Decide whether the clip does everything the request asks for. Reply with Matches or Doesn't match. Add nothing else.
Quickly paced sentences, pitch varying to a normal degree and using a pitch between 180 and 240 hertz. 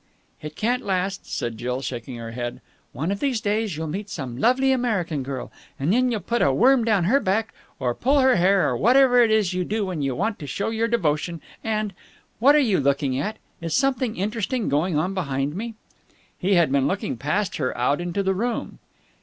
Doesn't match